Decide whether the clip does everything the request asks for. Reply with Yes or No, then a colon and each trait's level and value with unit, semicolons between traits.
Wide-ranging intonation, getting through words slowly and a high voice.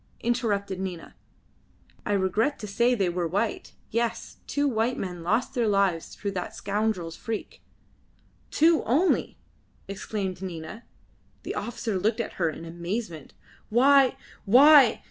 No: average, 4.4 semitones; slow, 130 wpm; high, 210 Hz